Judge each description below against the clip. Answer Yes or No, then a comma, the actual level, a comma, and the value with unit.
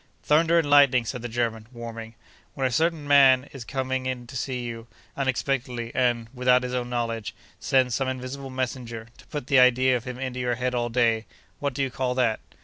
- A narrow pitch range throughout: Yes, narrow, 1.8 semitones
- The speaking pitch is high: No, low, 125 Hz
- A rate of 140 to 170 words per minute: No, average, 200 wpm